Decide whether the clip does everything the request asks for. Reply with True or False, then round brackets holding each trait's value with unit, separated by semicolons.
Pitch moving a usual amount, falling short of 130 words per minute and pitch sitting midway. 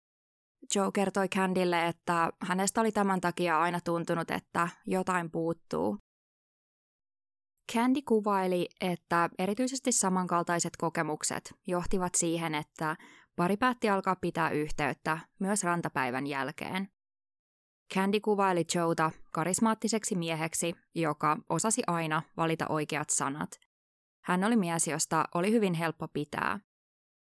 True (3.7 semitones; 110 wpm; 170 Hz)